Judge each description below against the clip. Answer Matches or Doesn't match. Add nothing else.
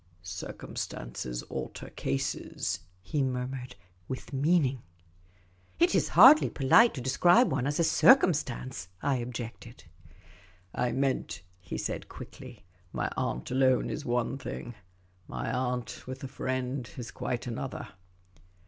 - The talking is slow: Matches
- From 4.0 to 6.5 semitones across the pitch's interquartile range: Doesn't match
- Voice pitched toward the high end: Doesn't match